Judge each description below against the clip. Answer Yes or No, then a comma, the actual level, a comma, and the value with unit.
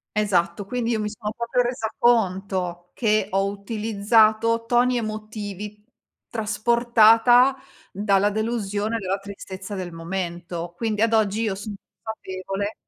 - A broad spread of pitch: No, average, 2.8 semitones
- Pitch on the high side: Yes, high, 210 Hz